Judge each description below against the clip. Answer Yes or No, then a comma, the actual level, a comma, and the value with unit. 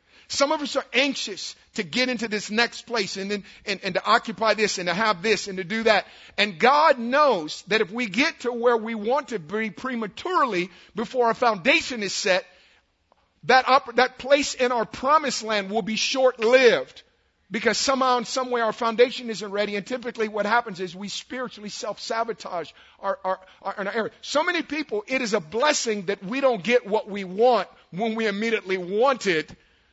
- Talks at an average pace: Yes, average, 195 wpm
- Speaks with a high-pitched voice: Yes, high, 225 Hz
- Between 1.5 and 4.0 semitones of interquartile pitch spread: Yes, average, 3.7 semitones